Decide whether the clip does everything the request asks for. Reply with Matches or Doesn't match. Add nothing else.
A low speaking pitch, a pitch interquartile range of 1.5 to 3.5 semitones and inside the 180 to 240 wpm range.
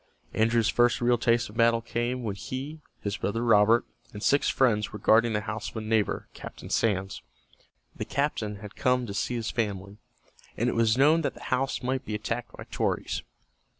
Matches